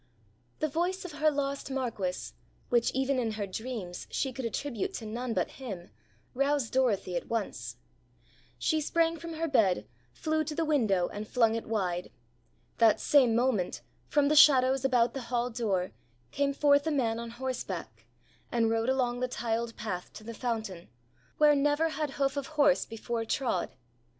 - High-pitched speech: Yes, high, 245 Hz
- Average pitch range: Yes, average, 4.4 semitones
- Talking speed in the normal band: Yes, average, 170 wpm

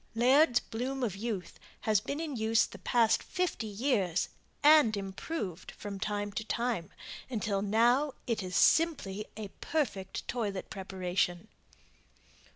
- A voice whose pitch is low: No, high, 220 Hz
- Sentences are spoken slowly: Yes, slow, 130 wpm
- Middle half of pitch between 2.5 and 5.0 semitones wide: Yes, average, 4.2 semitones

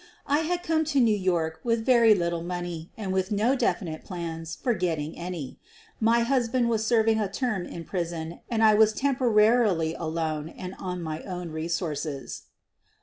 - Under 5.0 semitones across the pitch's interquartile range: No, wide, 5.6 semitones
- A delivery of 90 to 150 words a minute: No, average, 170 wpm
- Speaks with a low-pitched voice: No, high, 190 Hz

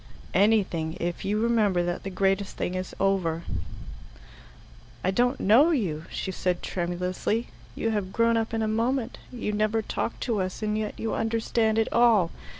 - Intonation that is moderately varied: Yes, average, 3.5 semitones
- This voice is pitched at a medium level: No, high, 210 Hz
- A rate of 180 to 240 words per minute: No, average, 165 wpm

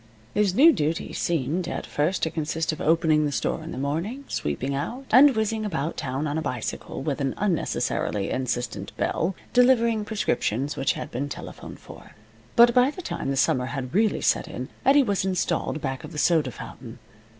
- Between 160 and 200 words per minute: Yes, average, 185 wpm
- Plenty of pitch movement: Yes, wide, 7.4 semitones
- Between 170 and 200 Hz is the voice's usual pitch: No, medium, 160 Hz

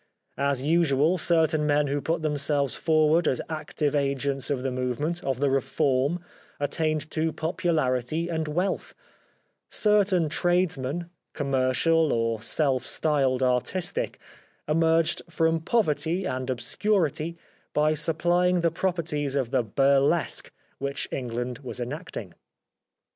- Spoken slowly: Yes, slow, 120 wpm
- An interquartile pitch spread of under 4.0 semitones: Yes, average, 3.5 semitones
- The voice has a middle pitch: Yes, medium, 150 Hz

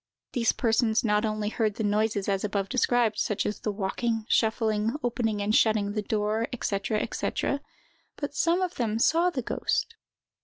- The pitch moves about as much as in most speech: No, narrow, 2.1 semitones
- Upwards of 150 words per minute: Yes, average, 165 wpm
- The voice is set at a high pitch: Yes, high, 220 Hz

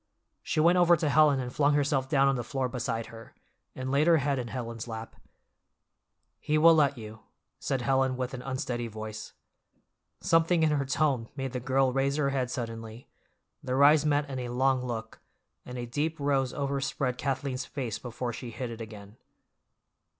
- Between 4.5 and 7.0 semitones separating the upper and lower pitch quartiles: No, average, 2.9 semitones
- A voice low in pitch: Yes, low, 130 Hz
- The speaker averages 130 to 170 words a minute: No, average, 180 wpm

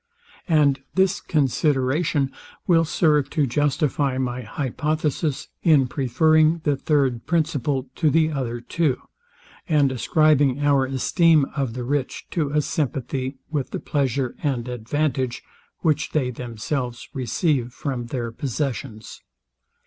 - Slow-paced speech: Yes, slow, 120 wpm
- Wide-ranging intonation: No, average, 3.2 semitones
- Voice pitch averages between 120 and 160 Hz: Yes, medium, 140 Hz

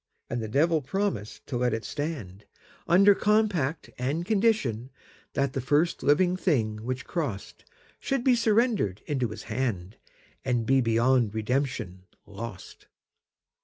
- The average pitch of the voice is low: Yes, low, 130 Hz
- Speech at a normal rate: No, slow, 115 wpm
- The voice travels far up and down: Yes, wide, 7.4 semitones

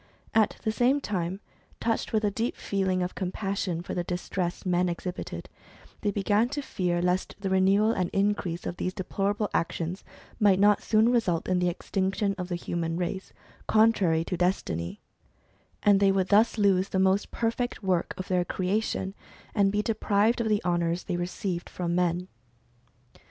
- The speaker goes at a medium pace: Yes, average, 165 wpm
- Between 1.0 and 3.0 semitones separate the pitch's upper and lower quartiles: Yes, average, 2.7 semitones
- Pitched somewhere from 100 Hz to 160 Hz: No, high, 190 Hz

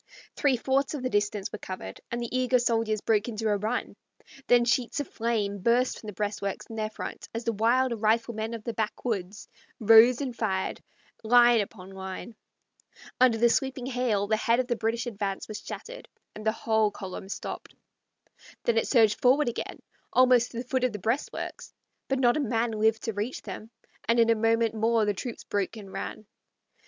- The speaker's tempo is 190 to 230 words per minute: Yes, average, 195 wpm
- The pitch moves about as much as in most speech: No, narrow, 2.3 semitones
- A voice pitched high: Yes, high, 225 Hz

